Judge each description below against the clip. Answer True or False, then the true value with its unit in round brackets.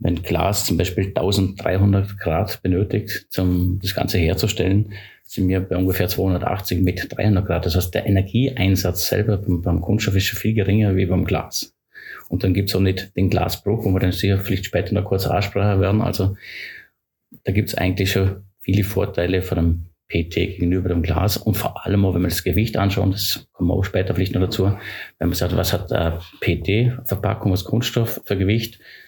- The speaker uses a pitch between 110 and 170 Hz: False (95 Hz)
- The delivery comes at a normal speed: False (195 wpm)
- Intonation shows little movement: True (2.1 semitones)